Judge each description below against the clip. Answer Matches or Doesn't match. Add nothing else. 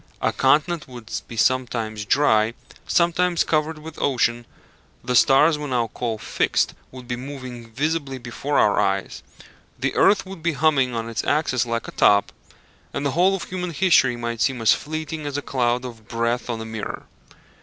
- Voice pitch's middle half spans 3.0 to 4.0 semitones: Doesn't match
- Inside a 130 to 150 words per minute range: Doesn't match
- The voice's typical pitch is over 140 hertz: Doesn't match